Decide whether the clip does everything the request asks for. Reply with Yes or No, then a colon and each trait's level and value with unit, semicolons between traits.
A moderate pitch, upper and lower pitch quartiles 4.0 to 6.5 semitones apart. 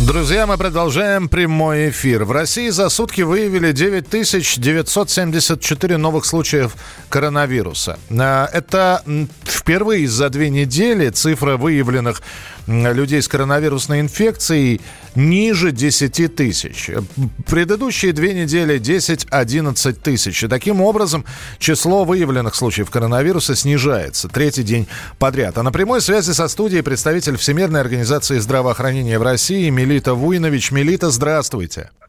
Yes: medium, 150 Hz; average, 5.2 semitones